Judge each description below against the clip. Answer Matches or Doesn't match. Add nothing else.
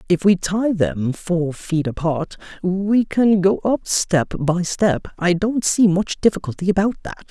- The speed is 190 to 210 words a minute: Doesn't match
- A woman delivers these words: Doesn't match